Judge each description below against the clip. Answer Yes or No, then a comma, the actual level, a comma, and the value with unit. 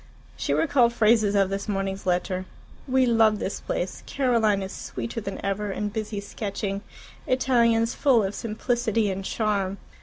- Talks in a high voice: Yes, high, 210 Hz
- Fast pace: No, average, 150 wpm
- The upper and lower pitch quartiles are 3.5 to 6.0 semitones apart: No, average, 2.9 semitones